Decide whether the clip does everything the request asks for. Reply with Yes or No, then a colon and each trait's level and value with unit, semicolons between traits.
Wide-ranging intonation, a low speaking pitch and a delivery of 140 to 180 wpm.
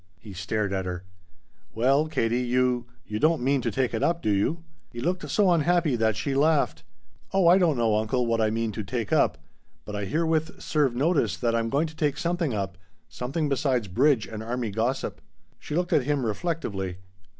No: wide, 6.0 semitones; low, 125 Hz; average, 195 wpm